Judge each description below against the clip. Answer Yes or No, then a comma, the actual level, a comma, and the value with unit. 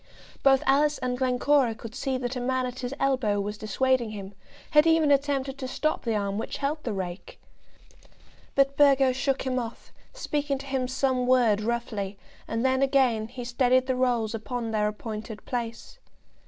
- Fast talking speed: No, average, 175 wpm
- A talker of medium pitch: No, very high, 255 Hz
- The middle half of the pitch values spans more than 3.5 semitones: No, average, 3.2 semitones